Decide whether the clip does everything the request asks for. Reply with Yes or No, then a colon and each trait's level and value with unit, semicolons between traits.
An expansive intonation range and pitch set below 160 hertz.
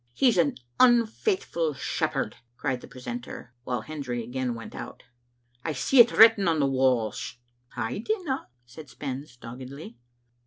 Yes: wide, 6.7 semitones; low, 135 Hz